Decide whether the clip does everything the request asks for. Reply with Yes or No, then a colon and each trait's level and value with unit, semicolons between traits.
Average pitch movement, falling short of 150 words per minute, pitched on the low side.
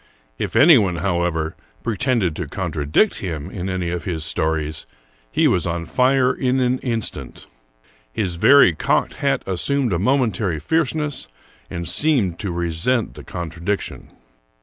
No: wide, 7.2 semitones; slow, 135 wpm; very low, 95 Hz